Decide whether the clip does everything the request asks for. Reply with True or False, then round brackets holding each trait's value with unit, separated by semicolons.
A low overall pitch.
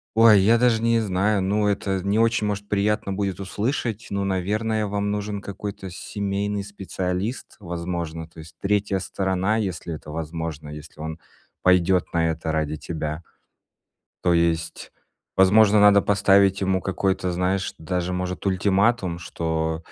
True (95 Hz)